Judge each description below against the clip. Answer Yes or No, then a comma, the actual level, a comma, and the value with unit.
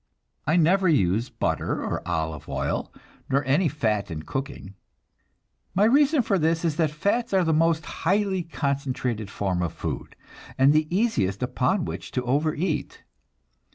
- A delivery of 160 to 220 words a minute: No, average, 150 wpm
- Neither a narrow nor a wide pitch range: No, wide, 6.4 semitones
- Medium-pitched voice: Yes, medium, 150 Hz